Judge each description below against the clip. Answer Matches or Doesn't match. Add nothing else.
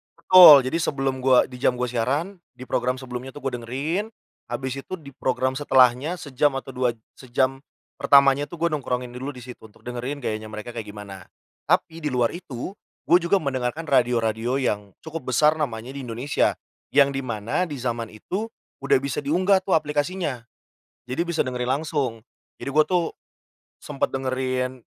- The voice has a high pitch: Doesn't match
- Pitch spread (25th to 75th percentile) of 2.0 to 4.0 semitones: Matches